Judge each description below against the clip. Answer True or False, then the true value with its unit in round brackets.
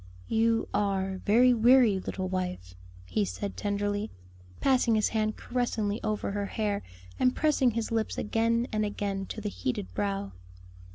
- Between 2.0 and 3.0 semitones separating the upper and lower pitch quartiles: True (2.7 semitones)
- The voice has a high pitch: True (210 Hz)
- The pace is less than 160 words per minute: True (150 wpm)